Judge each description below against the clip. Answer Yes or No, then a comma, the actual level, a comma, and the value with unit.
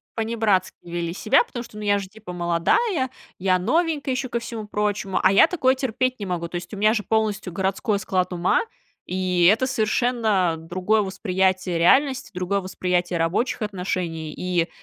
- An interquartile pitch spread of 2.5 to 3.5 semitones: No, average, 4.0 semitones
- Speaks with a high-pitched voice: Yes, high, 195 Hz